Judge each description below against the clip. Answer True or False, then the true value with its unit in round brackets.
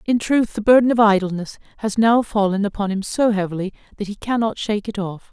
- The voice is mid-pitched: False (210 Hz)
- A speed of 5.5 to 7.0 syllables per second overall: True (6.0 syllables/s)